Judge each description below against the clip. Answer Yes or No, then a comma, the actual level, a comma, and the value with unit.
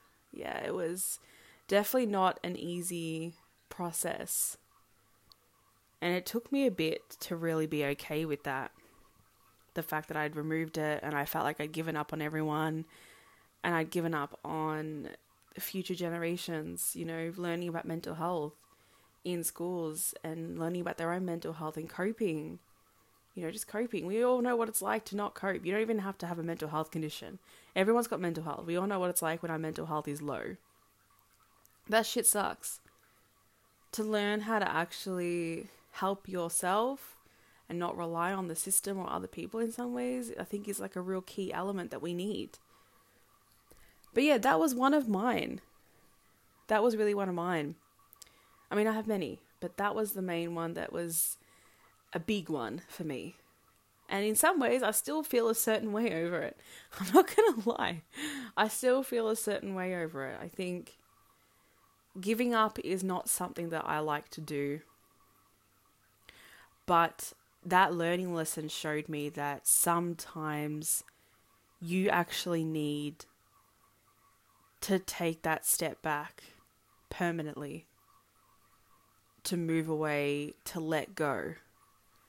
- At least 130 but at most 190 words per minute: Yes, average, 160 wpm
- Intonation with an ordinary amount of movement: Yes, average, 4.5 semitones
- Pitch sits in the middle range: Yes, medium, 175 Hz